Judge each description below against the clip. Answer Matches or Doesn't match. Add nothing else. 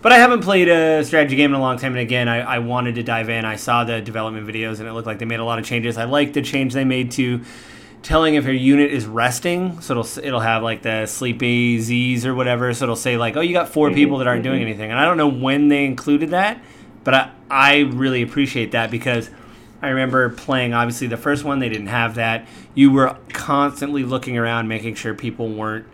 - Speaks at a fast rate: Matches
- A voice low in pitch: Matches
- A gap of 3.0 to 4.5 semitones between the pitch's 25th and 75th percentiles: Matches